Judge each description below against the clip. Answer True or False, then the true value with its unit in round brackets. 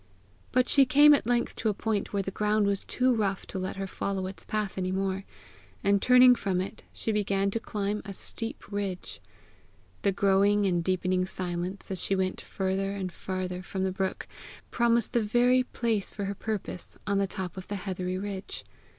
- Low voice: False (195 Hz)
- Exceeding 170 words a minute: True (195 wpm)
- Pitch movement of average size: False (2.2 semitones)